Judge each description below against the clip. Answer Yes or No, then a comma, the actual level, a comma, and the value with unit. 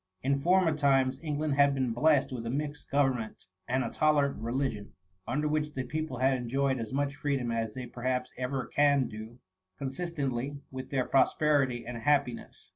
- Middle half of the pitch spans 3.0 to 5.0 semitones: No, narrow, 2.6 semitones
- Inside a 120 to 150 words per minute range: No, average, 175 wpm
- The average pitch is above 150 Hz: No, low, 135 Hz